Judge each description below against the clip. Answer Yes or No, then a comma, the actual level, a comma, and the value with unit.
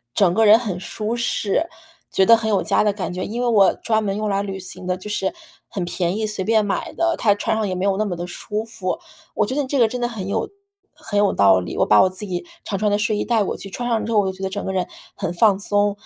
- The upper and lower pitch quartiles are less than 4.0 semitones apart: Yes, narrow, 2.6 semitones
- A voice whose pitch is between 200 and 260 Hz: Yes, high, 205 Hz